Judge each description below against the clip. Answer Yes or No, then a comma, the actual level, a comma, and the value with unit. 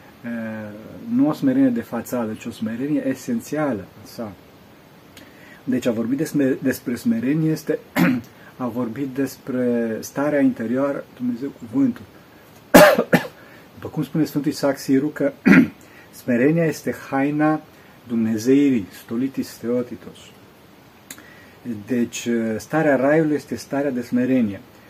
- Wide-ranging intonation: No, average, 4.2 semitones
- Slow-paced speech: Yes, slow, 110 wpm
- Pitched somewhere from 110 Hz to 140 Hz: Yes, low, 135 Hz